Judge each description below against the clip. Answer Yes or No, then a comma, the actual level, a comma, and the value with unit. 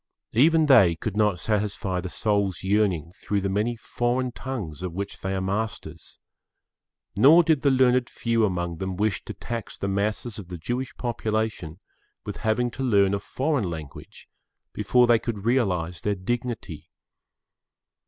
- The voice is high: No, low, 105 Hz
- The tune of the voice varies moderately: Yes, average, 4.2 semitones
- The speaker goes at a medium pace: Yes, average, 160 wpm